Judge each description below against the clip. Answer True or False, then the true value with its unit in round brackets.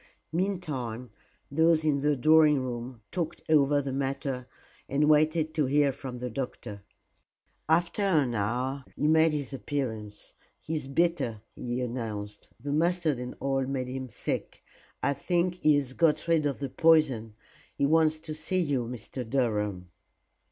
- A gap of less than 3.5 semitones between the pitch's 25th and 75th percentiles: False (4.0 semitones)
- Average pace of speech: True (150 wpm)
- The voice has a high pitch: False (140 Hz)